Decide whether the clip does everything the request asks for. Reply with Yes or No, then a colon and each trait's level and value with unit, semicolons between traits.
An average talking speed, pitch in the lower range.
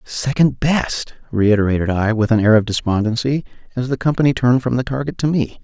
Yes: average, 190 wpm; low, 120 Hz